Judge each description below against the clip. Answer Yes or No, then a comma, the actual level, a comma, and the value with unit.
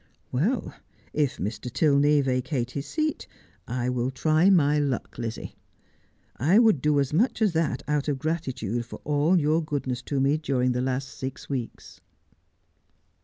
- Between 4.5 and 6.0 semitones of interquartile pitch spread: No, average, 3.5 semitones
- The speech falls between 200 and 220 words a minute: No, average, 155 wpm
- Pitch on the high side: No, medium, 140 Hz